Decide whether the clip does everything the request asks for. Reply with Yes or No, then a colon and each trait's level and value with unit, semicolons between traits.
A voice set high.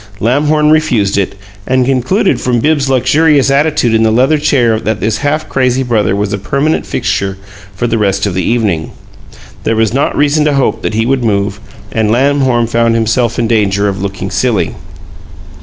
No: low, 120 Hz